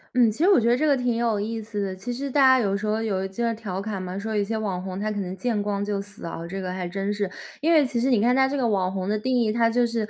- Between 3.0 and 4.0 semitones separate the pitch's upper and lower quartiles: Yes, average, 3.5 semitones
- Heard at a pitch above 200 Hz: Yes, high, 215 Hz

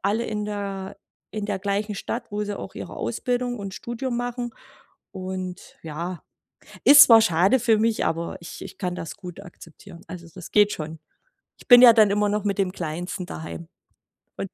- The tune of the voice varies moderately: Yes, average, 3.8 semitones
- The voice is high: Yes, high, 200 Hz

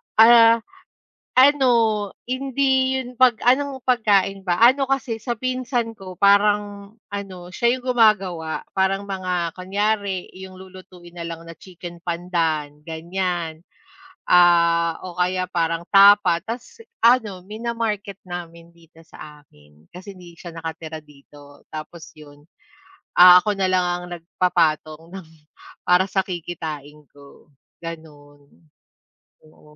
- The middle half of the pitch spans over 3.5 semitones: Yes, average, 4.2 semitones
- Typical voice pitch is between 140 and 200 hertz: Yes, medium, 185 Hz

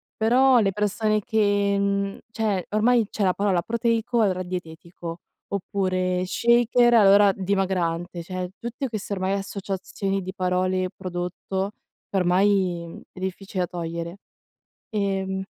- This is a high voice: Yes, high, 195 Hz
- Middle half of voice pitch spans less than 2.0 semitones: No, narrow, 2.4 semitones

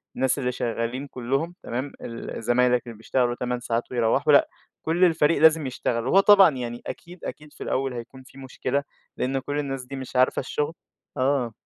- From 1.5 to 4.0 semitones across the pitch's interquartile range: Yes, average, 2.8 semitones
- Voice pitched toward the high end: No, low, 130 Hz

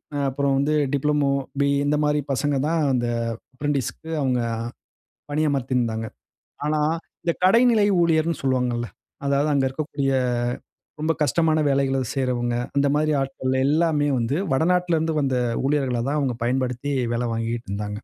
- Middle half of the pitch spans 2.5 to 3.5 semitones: Yes, average, 3.0 semitones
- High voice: No, medium, 140 Hz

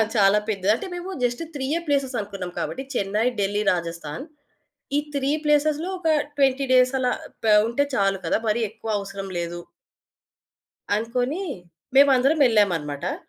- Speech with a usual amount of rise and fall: No, wide, 5.8 semitones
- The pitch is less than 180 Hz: No, high, 235 Hz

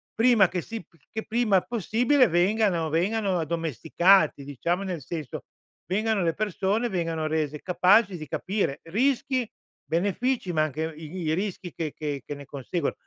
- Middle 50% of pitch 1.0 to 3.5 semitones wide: No, average, 5.2 semitones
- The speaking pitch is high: No, medium, 180 Hz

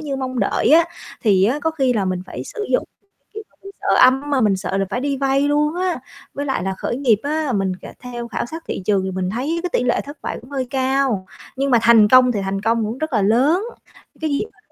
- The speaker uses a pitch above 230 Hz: Yes, very high, 255 Hz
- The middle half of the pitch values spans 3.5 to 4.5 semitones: No, average, 5.2 semitones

